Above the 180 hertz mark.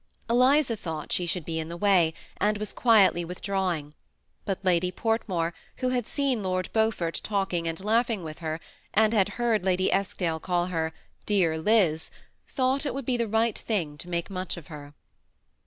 Yes: high, 190 Hz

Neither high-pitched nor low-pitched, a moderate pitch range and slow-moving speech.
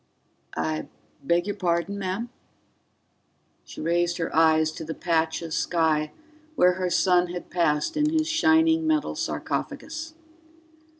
No: medium, 175 Hz; wide, 7.8 semitones; slow, 130 wpm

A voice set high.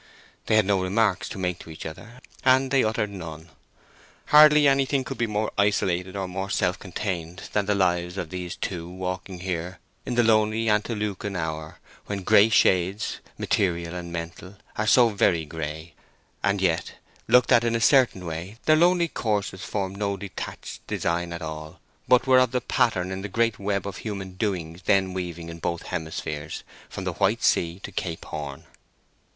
No: very low, 95 Hz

